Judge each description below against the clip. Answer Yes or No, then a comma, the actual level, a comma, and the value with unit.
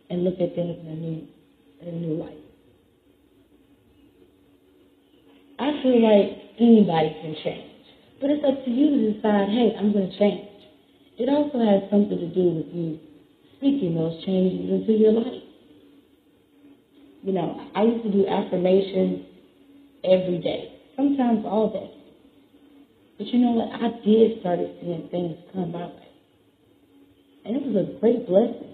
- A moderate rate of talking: Yes, average, 150 wpm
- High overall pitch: Yes, high, 200 Hz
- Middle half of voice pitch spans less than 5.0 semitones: No, wide, 5.4 semitones